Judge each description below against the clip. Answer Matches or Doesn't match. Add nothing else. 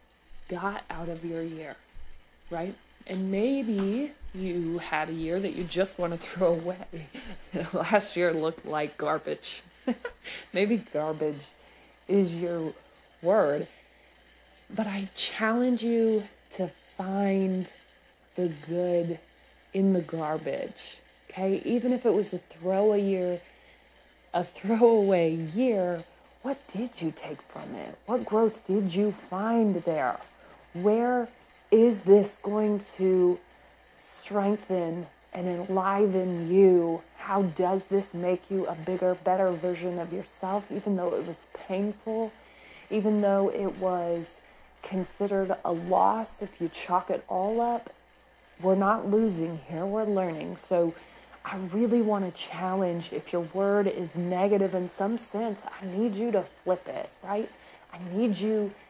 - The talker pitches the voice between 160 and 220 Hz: Matches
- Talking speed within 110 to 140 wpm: Matches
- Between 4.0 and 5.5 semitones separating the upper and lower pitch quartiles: Doesn't match